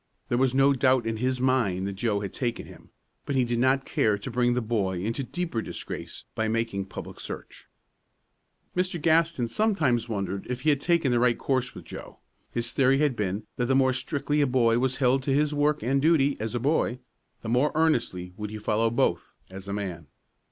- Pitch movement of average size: Yes, average, 3.7 semitones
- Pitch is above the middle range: No, low, 125 Hz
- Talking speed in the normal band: No, fast, 210 wpm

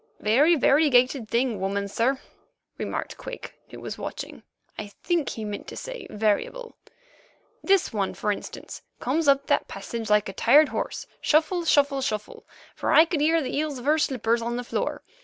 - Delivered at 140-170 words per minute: Yes, average, 165 wpm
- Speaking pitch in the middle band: No, very high, 265 Hz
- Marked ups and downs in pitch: Yes, wide, 6.1 semitones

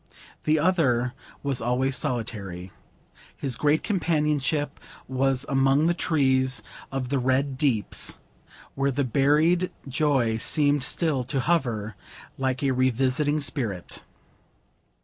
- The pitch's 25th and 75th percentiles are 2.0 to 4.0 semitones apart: Yes, average, 2.8 semitones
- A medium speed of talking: No, slow, 110 wpm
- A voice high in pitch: No, low, 135 Hz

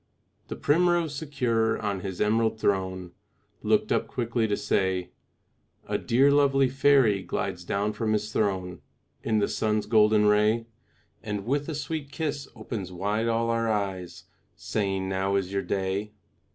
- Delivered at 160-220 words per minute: No, average, 150 wpm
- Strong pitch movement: No, average, 4.2 semitones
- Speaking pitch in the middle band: No, low, 110 Hz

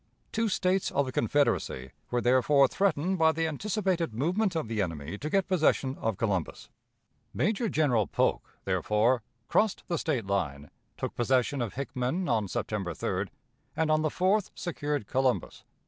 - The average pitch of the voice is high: No, medium, 140 Hz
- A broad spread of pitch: Yes, wide, 7.5 semitones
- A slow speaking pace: No, average, 155 wpm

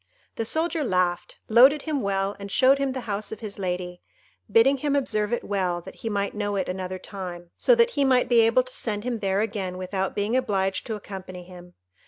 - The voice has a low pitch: No, high, 205 Hz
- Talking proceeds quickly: Yes, fast, 215 wpm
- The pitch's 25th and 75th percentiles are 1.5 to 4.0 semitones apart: No, average, 5.0 semitones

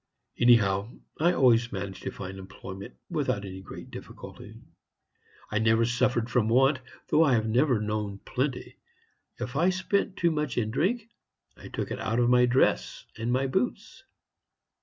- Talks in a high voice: No, low, 120 Hz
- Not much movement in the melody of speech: No, average, 4.3 semitones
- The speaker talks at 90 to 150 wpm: No, average, 160 wpm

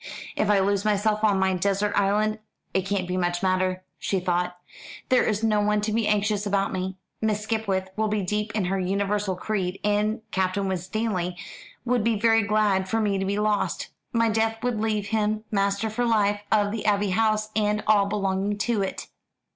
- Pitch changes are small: Yes, narrow, 1.9 semitones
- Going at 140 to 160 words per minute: No, average, 185 wpm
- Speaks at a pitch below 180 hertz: No, high, 205 Hz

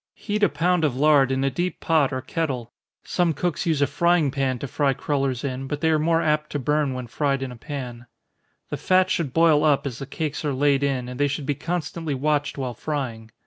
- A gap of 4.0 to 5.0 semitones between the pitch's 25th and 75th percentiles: No, average, 3.1 semitones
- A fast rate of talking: Yes, fast, 230 wpm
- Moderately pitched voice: Yes, medium, 145 Hz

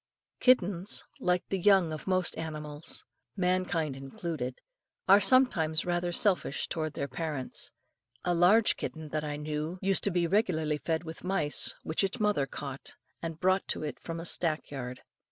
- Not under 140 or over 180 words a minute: Yes, average, 160 wpm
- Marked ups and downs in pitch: No, average, 3.4 semitones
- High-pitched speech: No, medium, 165 Hz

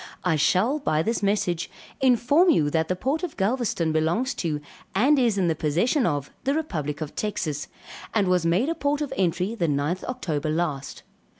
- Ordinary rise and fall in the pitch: No, wide, 8.1 semitones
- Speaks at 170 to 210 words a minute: Yes, average, 185 wpm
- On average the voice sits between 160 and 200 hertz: Yes, medium, 185 Hz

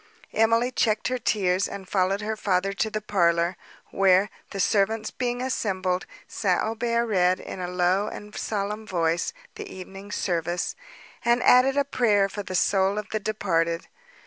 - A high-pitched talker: Yes, high, 200 Hz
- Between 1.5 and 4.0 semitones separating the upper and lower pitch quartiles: Yes, average, 3.0 semitones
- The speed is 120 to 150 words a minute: No, average, 160 wpm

